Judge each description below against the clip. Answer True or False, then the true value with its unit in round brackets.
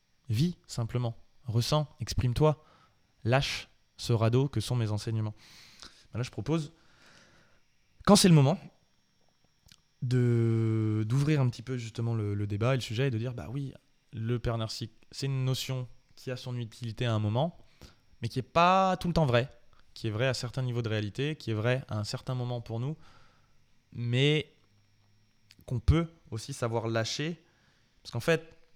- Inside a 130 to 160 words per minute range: False (170 wpm)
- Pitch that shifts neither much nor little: True (3.7 semitones)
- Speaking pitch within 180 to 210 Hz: False (120 Hz)